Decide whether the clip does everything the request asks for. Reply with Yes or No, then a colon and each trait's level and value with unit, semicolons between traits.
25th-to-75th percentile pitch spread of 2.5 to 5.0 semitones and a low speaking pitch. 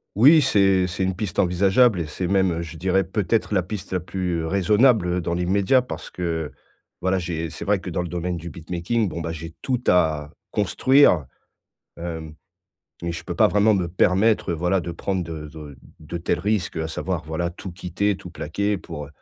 Yes: average, 2.9 semitones; very low, 90 Hz